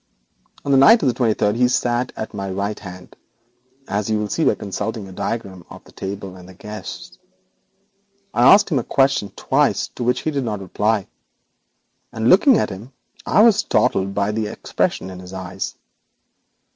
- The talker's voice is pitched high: No, low, 105 Hz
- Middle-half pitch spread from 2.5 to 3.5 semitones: No, average, 4.4 semitones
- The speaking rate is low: No, average, 185 wpm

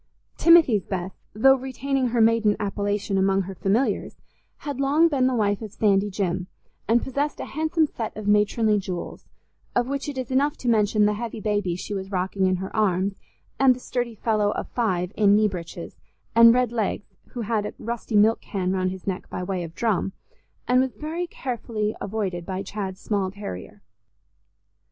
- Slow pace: No, average, 185 wpm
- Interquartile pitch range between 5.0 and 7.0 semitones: No, average, 4.1 semitones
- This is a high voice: Yes, high, 210 Hz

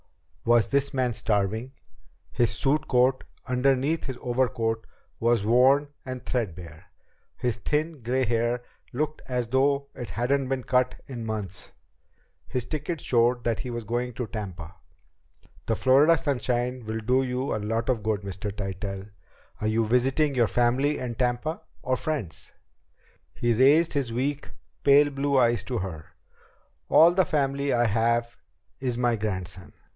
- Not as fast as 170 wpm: Yes, average, 150 wpm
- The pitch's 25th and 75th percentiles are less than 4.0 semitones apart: Yes, average, 3.2 semitones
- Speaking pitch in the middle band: No, low, 125 Hz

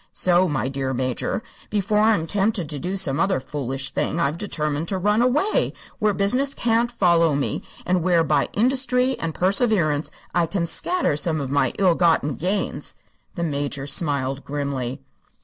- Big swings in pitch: Yes, wide, 6.1 semitones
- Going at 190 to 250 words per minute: No, average, 165 wpm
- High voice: No, medium, 170 Hz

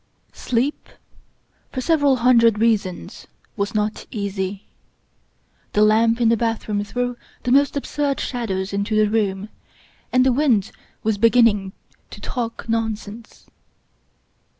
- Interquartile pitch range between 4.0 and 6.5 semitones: No, average, 3.0 semitones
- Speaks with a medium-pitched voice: No, high, 225 Hz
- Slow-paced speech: Yes, slow, 125 wpm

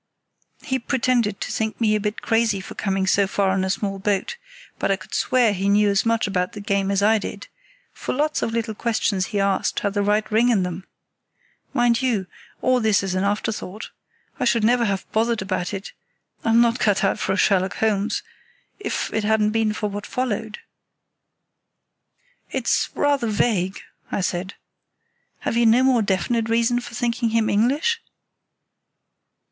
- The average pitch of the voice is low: No, high, 215 Hz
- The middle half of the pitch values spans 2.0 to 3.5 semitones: Yes, average, 2.9 semitones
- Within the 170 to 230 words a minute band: Yes, average, 175 wpm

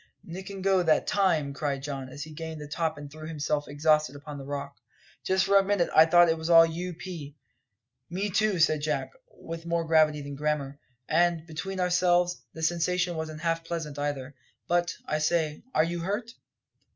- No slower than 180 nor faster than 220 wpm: Yes, average, 190 wpm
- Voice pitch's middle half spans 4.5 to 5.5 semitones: No, average, 2.8 semitones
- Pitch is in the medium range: Yes, medium, 160 Hz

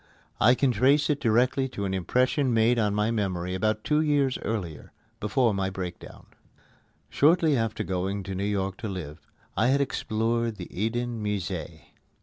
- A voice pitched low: Yes, low, 110 Hz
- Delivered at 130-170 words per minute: Yes, average, 160 wpm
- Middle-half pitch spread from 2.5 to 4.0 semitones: No, average, 4.6 semitones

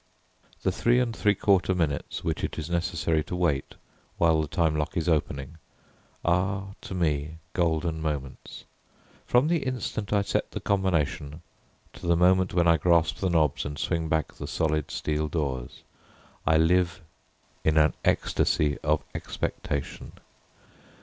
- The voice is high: No, very low, 80 Hz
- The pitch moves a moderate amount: Yes, average, 3.1 semitones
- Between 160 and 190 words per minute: No, average, 150 wpm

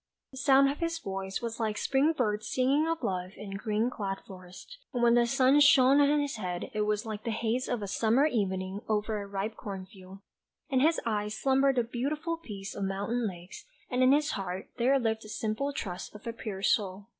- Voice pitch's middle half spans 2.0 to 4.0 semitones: No, average, 5.1 semitones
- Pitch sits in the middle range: No, high, 220 Hz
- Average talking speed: No, fast, 210 wpm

